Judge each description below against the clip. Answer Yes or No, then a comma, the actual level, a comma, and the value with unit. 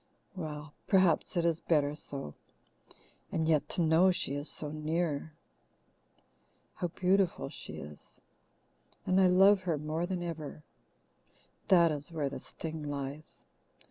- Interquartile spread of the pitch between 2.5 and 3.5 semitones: Yes, average, 3.0 semitones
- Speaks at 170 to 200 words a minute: No, slow, 135 wpm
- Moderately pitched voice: Yes, medium, 160 Hz